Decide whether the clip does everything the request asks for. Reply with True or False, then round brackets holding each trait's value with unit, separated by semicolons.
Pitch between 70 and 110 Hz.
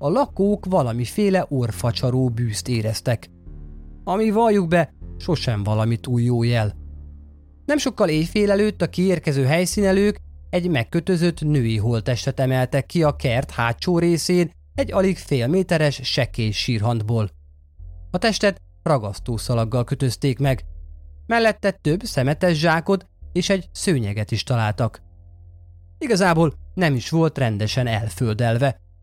False (130 Hz)